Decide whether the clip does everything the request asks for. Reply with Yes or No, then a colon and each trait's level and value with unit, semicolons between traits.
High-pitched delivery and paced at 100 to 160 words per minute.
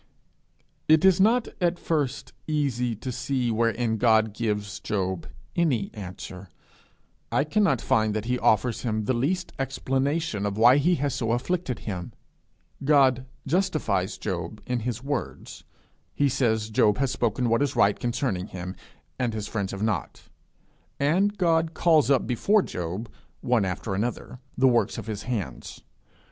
No: low, 120 Hz; average, 150 wpm